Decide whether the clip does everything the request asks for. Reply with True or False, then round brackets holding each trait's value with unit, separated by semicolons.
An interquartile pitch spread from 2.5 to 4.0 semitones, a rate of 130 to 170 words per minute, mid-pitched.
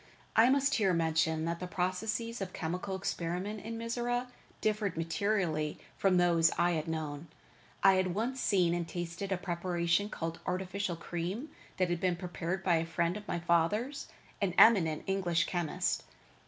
True (3.3 semitones; 160 wpm; 180 Hz)